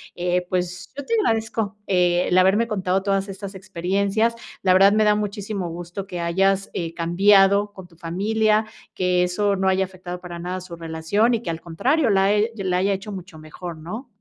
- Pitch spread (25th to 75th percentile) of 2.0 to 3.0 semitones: Yes, narrow, 2.6 semitones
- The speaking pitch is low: No, high, 190 Hz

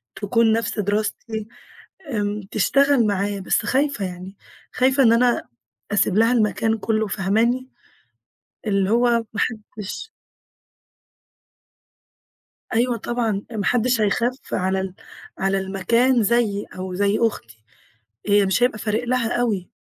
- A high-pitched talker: Yes, high, 215 Hz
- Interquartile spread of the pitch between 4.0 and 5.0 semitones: No, average, 3.2 semitones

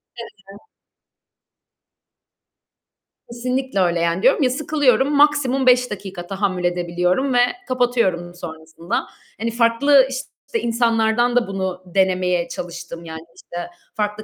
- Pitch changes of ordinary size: No, wide, 6.1 semitones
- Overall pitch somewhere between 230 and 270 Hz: No, high, 210 Hz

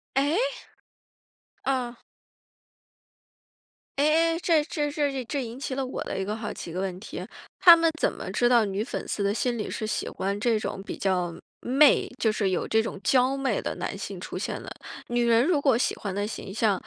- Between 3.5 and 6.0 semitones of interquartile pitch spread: Yes, average, 5.1 semitones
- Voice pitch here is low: No, high, 235 Hz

